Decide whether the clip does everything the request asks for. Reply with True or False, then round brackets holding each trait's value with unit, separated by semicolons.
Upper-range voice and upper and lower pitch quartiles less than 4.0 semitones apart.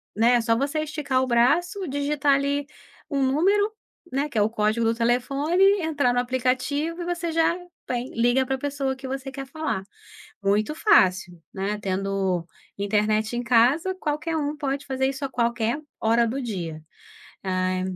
False (260 Hz; 4.5 semitones)